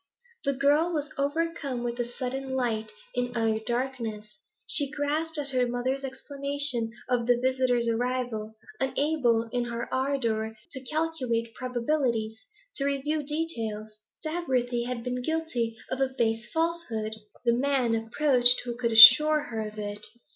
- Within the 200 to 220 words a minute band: No, average, 140 wpm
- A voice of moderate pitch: No, very high, 250 Hz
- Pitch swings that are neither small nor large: Yes, average, 3.3 semitones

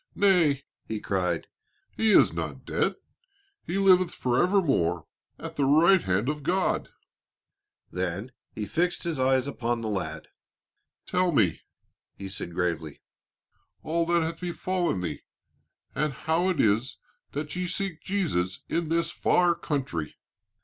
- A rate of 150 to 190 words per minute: No, slow, 135 wpm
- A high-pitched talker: No, medium, 145 Hz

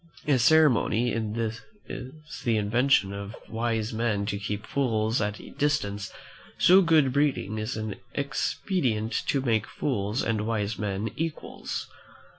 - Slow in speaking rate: Yes, slow, 130 wpm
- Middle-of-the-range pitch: No, low, 115 Hz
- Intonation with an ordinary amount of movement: Yes, average, 4.6 semitones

